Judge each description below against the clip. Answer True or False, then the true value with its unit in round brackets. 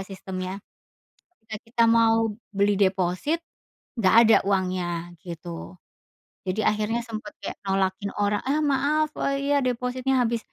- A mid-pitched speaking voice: False (205 Hz)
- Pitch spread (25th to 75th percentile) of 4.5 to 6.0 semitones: False (4.0 semitones)